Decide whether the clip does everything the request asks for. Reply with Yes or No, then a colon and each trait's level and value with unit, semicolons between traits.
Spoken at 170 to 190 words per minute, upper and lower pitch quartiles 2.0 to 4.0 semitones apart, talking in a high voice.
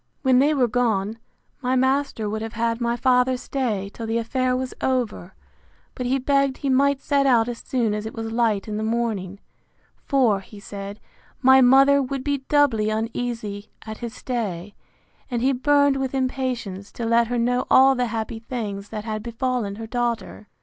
Yes: average, 185 wpm; average, 3.1 semitones; high, 235 Hz